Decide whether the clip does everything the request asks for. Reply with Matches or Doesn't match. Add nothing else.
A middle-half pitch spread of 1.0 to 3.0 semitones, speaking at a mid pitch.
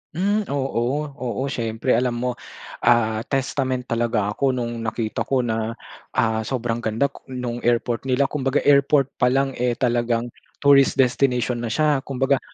Doesn't match